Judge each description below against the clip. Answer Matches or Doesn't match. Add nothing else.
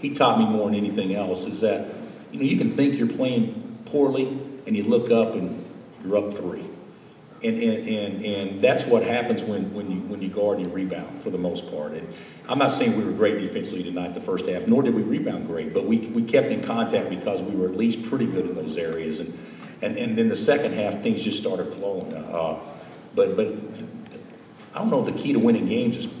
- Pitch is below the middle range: Matches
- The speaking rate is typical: Doesn't match